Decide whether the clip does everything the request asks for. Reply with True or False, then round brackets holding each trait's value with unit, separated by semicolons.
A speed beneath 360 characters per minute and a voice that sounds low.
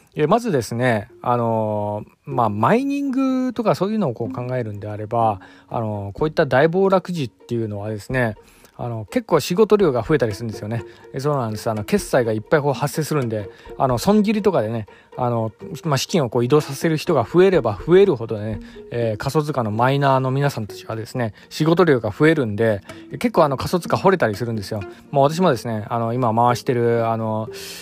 False (410 characters per minute; 125 Hz)